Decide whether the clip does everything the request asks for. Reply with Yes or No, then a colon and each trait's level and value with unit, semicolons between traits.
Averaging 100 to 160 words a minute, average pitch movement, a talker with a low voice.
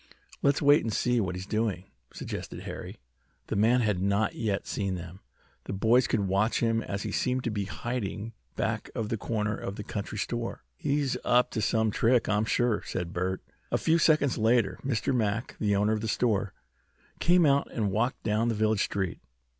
No: average, 195 wpm; average, 3.2 semitones; low, 110 Hz